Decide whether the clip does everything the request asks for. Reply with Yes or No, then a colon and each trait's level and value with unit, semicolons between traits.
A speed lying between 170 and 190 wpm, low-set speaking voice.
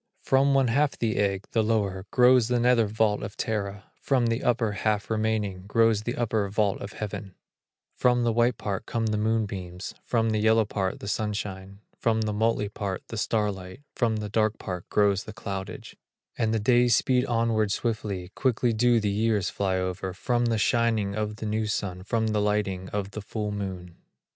Yes: average, 185 wpm; low, 110 Hz